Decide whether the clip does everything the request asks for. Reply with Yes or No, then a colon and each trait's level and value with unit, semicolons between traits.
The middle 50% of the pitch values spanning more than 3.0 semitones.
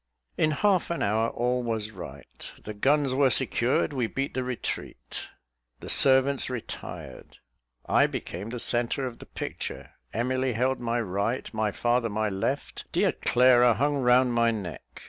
No: average, 2.7 semitones